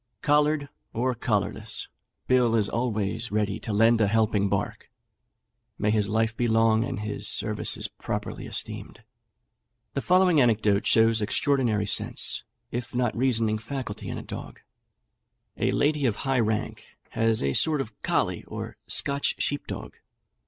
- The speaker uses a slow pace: No, average, 145 wpm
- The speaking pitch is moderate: No, low, 115 Hz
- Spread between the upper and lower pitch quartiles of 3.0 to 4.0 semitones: Yes, average, 3.4 semitones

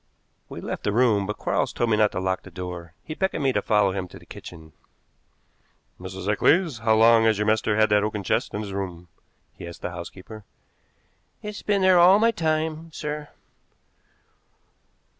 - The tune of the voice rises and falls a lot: Yes, wide, 8.2 semitones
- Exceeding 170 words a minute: Yes, average, 185 wpm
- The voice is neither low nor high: No, low, 110 Hz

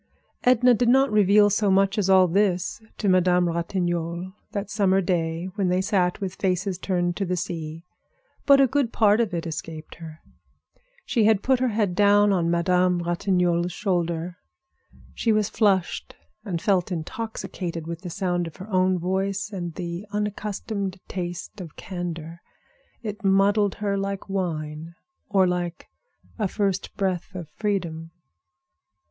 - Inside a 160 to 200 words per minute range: No, average, 150 wpm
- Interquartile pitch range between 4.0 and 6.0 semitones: No, average, 2.7 semitones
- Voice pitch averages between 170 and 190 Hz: Yes, medium, 185 Hz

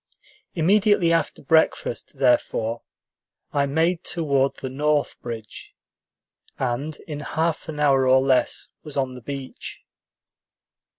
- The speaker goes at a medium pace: No, slow, 115 wpm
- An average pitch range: Yes, average, 3.4 semitones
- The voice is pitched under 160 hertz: Yes, medium, 140 Hz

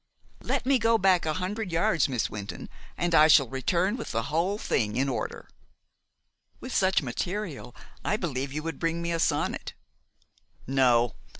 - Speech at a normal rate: Yes, average, 165 wpm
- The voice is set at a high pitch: No, medium, 165 Hz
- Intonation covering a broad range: Yes, wide, 6.1 semitones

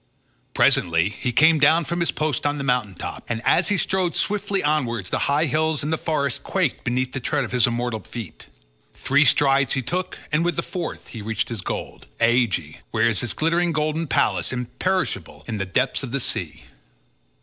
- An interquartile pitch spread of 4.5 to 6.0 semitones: Yes, average, 5.2 semitones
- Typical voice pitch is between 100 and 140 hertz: Yes, low, 135 Hz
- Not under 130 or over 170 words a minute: No, average, 195 wpm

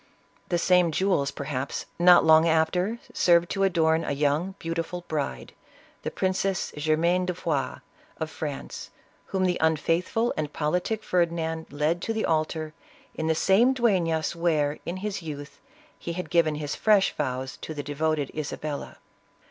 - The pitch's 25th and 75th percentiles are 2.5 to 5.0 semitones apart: Yes, average, 3.0 semitones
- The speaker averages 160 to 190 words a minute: No, average, 150 wpm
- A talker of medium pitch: Yes, medium, 165 Hz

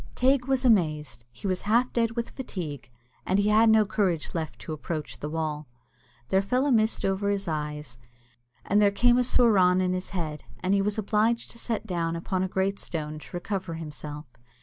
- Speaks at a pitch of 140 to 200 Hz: Yes, high, 190 Hz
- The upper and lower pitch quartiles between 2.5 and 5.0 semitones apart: No, wide, 5.5 semitones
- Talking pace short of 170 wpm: No, average, 195 wpm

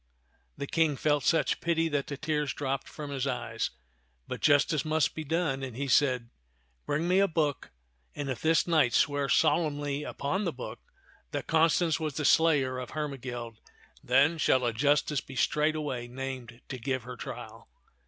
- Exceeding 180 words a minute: No, average, 175 wpm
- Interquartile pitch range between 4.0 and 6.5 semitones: No, average, 3.2 semitones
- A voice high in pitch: No, medium, 145 Hz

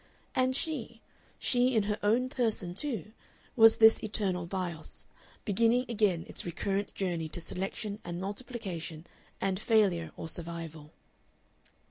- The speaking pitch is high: Yes, high, 200 Hz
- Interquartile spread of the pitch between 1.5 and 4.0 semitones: No, average, 4.7 semitones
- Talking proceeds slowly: Yes, slow, 125 wpm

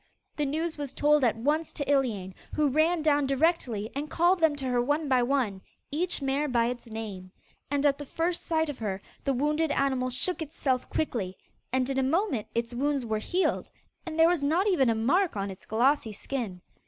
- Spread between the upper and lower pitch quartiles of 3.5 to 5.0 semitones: Yes, average, 4.6 semitones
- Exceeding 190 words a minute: Yes, fast, 205 wpm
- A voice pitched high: Yes, very high, 275 Hz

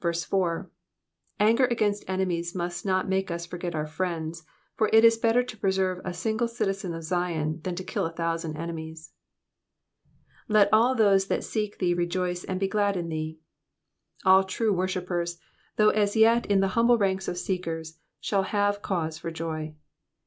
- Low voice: No, medium, 185 Hz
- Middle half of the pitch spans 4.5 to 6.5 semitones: No, average, 3.4 semitones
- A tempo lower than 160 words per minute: No, average, 165 wpm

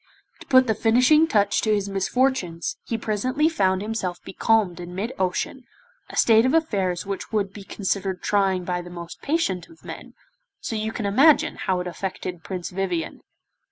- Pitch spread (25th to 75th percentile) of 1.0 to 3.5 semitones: No, average, 3.9 semitones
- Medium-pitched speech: No, high, 200 Hz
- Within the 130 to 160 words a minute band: No, average, 175 wpm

